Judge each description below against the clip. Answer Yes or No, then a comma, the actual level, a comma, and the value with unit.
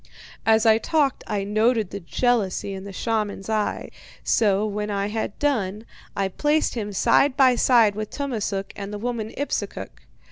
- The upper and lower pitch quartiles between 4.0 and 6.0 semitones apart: No, average, 3.3 semitones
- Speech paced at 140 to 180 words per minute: Yes, average, 165 wpm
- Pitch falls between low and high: No, high, 215 Hz